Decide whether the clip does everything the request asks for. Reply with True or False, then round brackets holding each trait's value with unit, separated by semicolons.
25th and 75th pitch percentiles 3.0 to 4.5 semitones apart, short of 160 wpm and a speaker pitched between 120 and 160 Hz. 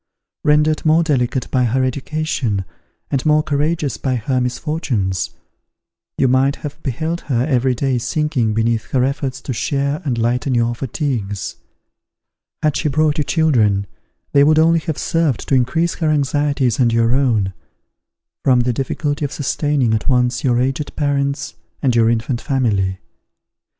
True (3.7 semitones; 150 wpm; 135 Hz)